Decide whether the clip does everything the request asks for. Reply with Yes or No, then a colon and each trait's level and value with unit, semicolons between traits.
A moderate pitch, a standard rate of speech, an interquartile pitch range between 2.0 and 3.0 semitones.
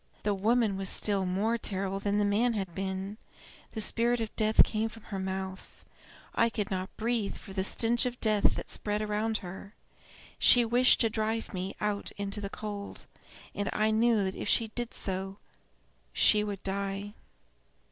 No: high, 210 Hz; average, 175 wpm; narrow, 2.4 semitones